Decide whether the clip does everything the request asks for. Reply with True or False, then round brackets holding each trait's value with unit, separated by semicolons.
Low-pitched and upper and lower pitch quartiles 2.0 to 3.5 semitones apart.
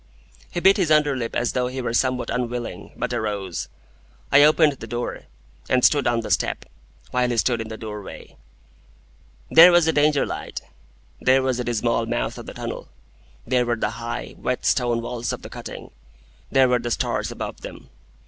True (125 Hz; 2.4 semitones)